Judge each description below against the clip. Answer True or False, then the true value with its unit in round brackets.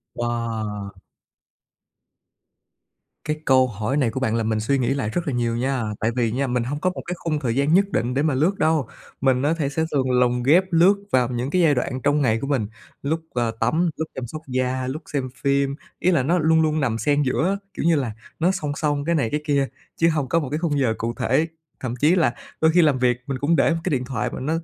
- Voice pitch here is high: False (140 Hz)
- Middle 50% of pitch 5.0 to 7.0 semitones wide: False (4.2 semitones)